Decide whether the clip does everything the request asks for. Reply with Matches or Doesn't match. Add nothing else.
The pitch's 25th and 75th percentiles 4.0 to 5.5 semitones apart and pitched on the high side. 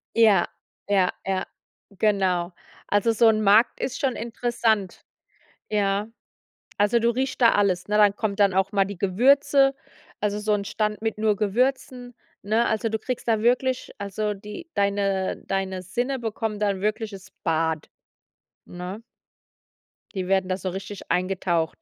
Doesn't match